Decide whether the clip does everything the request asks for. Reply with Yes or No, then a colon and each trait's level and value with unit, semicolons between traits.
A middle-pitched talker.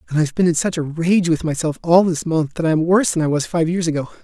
Yes: medium, 165 Hz